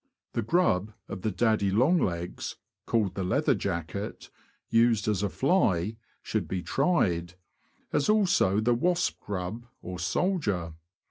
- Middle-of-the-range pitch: No, low, 105 Hz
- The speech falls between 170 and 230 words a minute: No, average, 145 wpm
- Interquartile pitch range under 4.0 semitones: No, average, 5.2 semitones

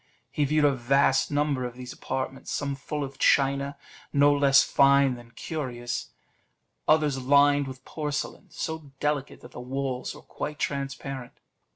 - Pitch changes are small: Yes, narrow, 1.6 semitones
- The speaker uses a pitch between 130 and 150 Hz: Yes, medium, 140 Hz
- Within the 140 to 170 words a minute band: Yes, average, 150 wpm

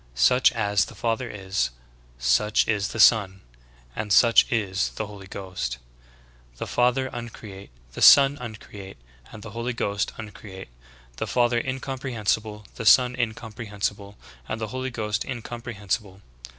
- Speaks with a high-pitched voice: No, low, 110 Hz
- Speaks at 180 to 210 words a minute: No, slow, 135 wpm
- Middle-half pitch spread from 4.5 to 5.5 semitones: No, average, 3.0 semitones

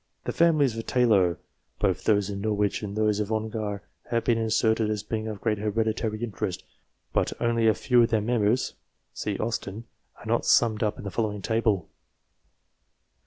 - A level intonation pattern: Yes, narrow, 1.7 semitones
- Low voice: Yes, low, 110 Hz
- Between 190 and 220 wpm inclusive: No, average, 165 wpm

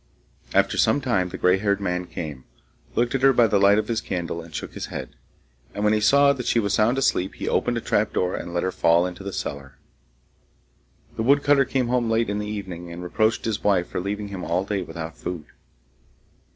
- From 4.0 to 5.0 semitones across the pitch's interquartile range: Yes, average, 4.5 semitones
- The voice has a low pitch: Yes, low, 100 Hz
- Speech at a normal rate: No, fast, 215 wpm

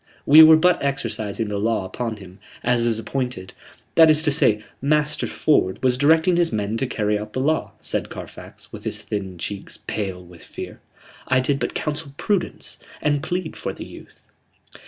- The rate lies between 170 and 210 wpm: Yes, average, 180 wpm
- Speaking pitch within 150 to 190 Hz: No, low, 125 Hz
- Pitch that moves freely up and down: Yes, wide, 6.4 semitones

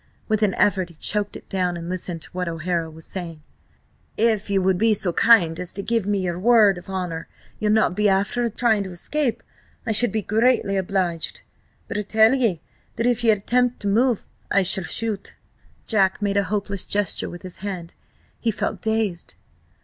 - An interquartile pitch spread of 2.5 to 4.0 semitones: Yes, average, 3.4 semitones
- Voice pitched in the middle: No, high, 200 Hz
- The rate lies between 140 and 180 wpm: No, average, 195 wpm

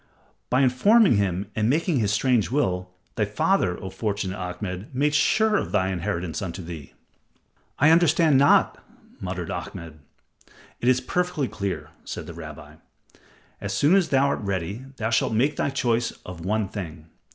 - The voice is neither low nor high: No, low, 105 Hz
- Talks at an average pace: Yes, average, 160 wpm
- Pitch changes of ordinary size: No, wide, 7.1 semitones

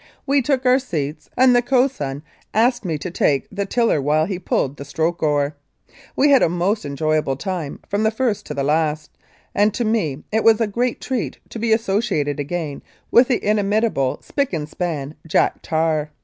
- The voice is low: No, medium, 185 Hz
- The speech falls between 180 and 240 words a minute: Yes, average, 185 wpm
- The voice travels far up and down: Yes, wide, 7.4 semitones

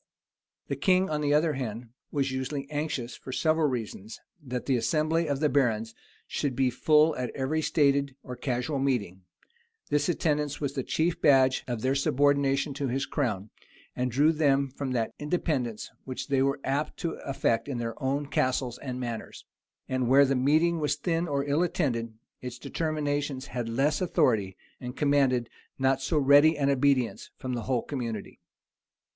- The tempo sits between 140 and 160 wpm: No, average, 170 wpm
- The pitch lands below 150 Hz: Yes, low, 135 Hz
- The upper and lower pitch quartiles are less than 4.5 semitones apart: Yes, average, 2.8 semitones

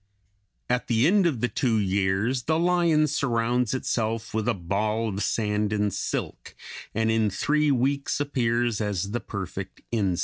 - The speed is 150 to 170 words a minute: Yes, average, 160 wpm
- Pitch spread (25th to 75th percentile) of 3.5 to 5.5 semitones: Yes, average, 4.1 semitones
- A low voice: Yes, low, 115 Hz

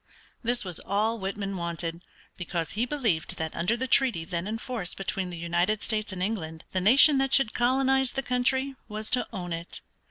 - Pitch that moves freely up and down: Yes, wide, 6.0 semitones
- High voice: Yes, high, 210 Hz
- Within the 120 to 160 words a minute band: No, average, 190 wpm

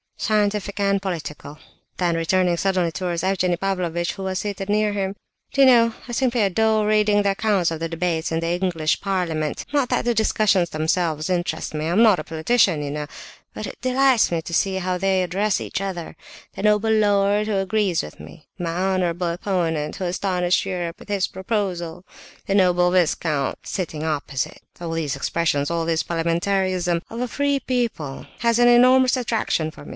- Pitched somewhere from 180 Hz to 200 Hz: Yes, medium, 185 Hz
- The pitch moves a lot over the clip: No, average, 3.8 semitones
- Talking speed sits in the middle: Yes, average, 180 wpm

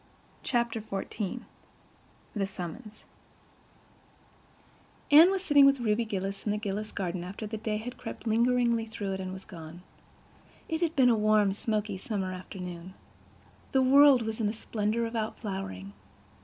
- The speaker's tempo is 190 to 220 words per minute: No, average, 155 wpm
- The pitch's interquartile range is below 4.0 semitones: Yes, average, 3.6 semitones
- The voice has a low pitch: No, high, 215 Hz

